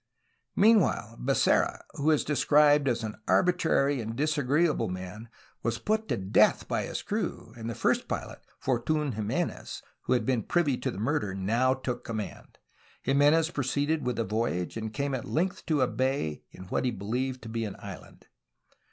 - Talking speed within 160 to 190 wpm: Yes, average, 175 wpm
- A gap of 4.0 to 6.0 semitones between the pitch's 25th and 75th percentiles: Yes, average, 4.9 semitones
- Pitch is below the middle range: Yes, low, 130 Hz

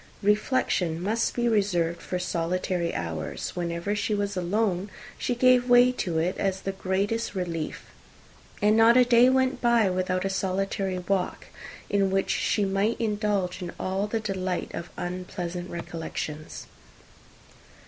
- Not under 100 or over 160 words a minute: Yes, average, 140 wpm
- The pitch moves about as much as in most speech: Yes, average, 3.2 semitones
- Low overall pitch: No, high, 195 Hz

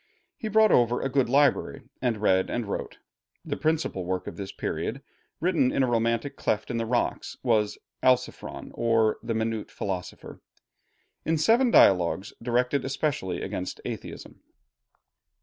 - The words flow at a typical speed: Yes, average, 145 wpm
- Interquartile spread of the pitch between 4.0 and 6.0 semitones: Yes, average, 4.5 semitones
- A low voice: Yes, low, 120 Hz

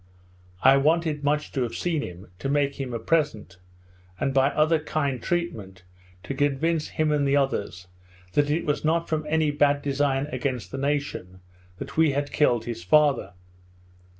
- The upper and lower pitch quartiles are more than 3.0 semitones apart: No, average, 2.7 semitones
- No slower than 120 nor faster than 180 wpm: Yes, average, 170 wpm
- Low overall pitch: No, medium, 145 Hz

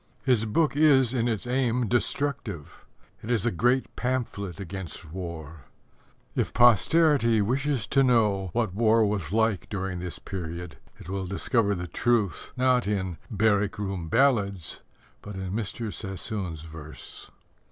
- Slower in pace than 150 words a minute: Yes, average, 140 wpm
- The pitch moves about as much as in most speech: Yes, average, 4.5 semitones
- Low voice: Yes, low, 105 Hz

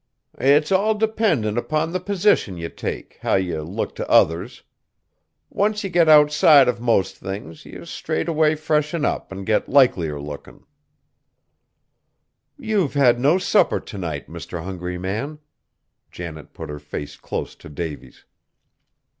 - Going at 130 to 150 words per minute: Yes, average, 140 wpm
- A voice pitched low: Yes, low, 125 Hz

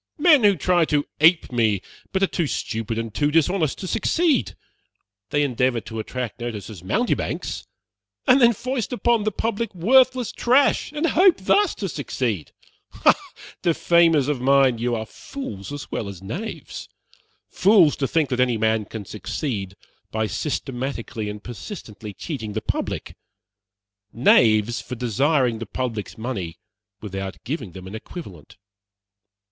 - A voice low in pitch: Yes, low, 130 Hz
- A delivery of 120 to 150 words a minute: Yes, average, 145 wpm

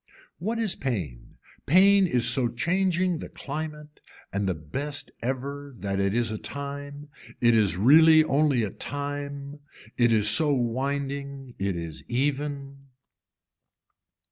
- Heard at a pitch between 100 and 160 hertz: Yes, medium, 140 Hz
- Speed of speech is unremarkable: No, slow, 130 wpm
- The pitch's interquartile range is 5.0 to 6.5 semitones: No, average, 4.0 semitones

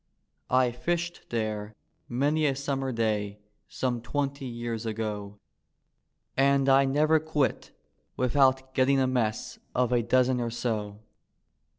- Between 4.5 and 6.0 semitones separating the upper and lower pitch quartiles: No, average, 3.3 semitones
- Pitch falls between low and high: No, low, 130 Hz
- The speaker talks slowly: Yes, slow, 120 wpm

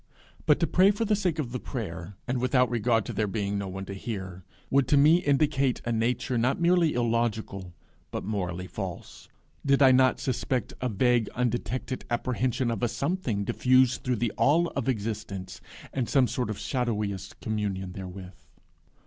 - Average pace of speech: Yes, average, 175 wpm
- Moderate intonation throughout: Yes, average, 4.6 semitones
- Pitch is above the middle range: No, low, 120 Hz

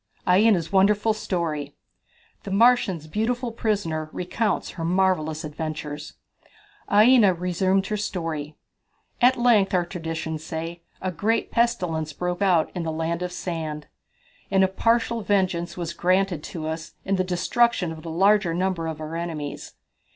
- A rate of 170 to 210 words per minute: No, average, 145 wpm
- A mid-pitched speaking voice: Yes, medium, 180 Hz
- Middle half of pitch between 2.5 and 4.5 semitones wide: Yes, average, 3.8 semitones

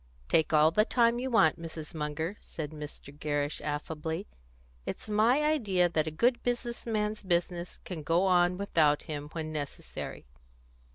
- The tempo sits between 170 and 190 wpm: No, average, 155 wpm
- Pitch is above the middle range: No, medium, 170 Hz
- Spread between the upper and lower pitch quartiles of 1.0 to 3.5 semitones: No, wide, 5.6 semitones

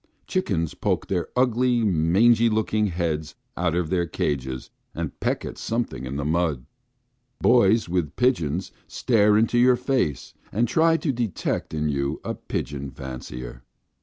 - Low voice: Yes, very low, 90 Hz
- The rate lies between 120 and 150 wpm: Yes, average, 145 wpm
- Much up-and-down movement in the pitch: Yes, wide, 7.7 semitones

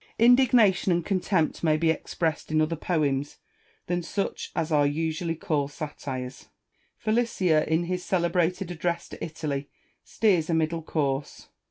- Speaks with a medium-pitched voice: Yes, medium, 165 Hz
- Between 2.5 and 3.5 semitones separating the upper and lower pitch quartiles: Yes, average, 2.8 semitones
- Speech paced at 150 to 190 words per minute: No, average, 140 wpm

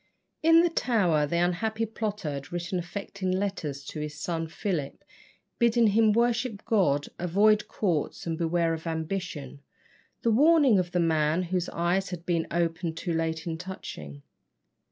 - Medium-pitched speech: Yes, medium, 175 Hz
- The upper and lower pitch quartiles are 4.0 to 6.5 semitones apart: Yes, average, 4.4 semitones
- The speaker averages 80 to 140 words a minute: No, average, 155 wpm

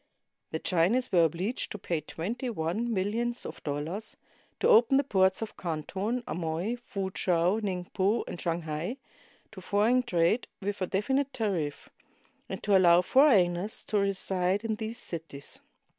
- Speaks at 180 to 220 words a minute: No, average, 145 wpm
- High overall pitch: Yes, high, 195 Hz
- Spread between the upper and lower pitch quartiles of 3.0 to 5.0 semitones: Yes, average, 4.7 semitones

